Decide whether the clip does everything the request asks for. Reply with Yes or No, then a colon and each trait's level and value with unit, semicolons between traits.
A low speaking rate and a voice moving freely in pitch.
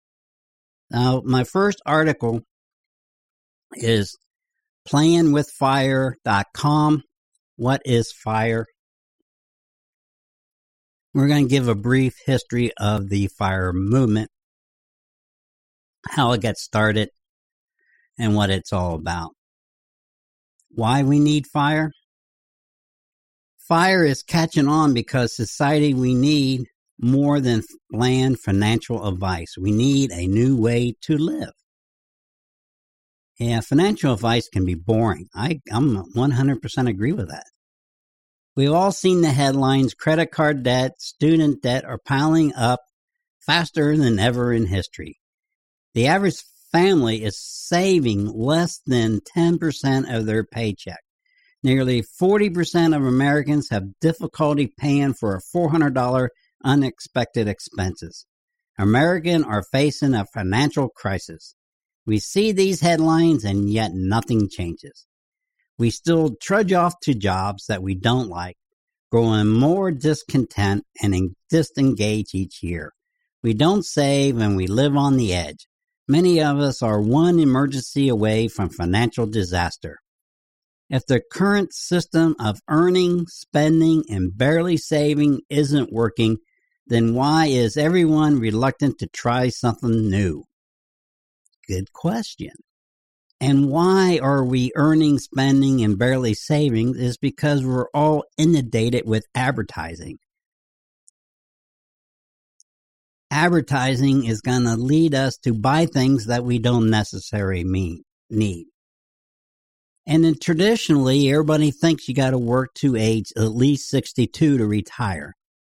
Yes: slow, 120 wpm; wide, 5.7 semitones